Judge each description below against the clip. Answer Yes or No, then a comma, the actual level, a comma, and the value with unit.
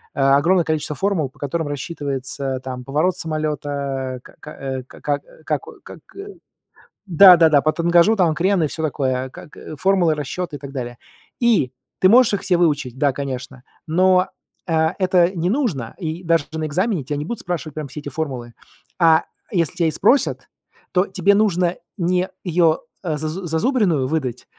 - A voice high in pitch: No, medium, 160 Hz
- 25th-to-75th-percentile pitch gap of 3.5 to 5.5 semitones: Yes, average, 4.5 semitones